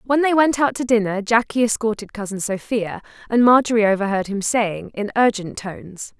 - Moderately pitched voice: No, high, 220 Hz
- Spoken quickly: No, average, 175 wpm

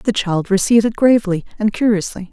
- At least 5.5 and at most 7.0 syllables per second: Yes, 6.1 syllables/s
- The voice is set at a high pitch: Yes, high, 205 Hz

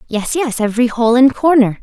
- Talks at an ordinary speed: Yes, average, 195 wpm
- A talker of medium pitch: No, high, 245 Hz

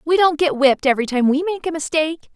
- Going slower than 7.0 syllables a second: No, 7.1 syllables/s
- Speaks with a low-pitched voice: No, very high, 305 Hz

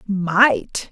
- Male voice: No, female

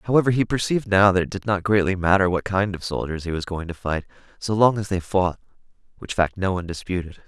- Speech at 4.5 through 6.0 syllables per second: No, 6.2 syllables/s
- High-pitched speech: No, very low, 95 Hz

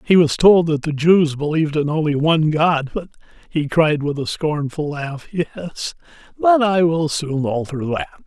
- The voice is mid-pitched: Yes, medium, 155 Hz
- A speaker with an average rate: Yes, average, 180 wpm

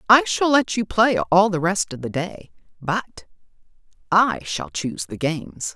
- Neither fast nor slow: Yes, average, 175 wpm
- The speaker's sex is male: No, female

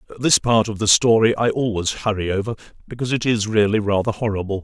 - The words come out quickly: No, average, 195 wpm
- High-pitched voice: No, low, 110 Hz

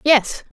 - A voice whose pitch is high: Yes, very high, 250 Hz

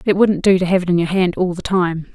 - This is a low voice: No, medium, 180 Hz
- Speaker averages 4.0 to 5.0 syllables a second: No, 6.1 syllables/s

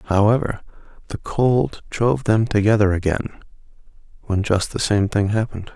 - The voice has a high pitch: No, low, 105 Hz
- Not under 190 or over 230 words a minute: No, slow, 135 wpm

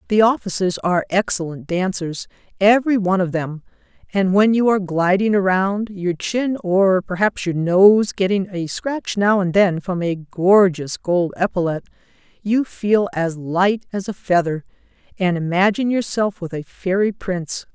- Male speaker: No, female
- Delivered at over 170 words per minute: No, average, 150 wpm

